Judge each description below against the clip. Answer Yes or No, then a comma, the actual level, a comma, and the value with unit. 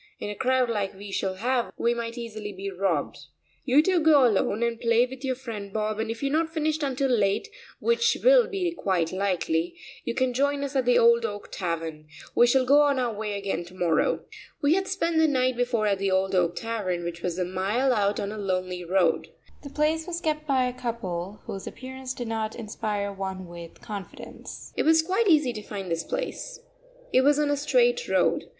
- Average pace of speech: No, fast, 215 wpm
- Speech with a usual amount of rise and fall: No, wide, 6.3 semitones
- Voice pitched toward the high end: Yes, high, 235 Hz